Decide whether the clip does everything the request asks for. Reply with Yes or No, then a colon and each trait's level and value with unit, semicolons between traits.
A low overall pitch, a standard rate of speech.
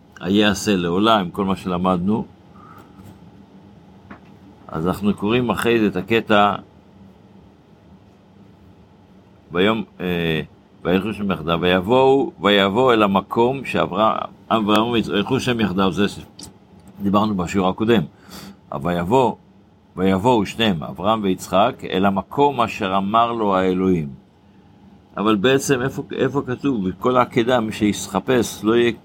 Yes: low, 100 Hz; average, 110 wpm